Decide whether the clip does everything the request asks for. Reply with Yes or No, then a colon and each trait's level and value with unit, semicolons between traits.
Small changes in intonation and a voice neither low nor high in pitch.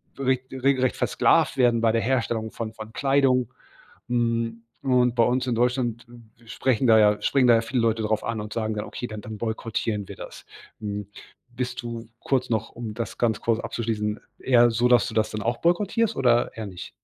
No: narrow, 2.2 semitones; low, 115 Hz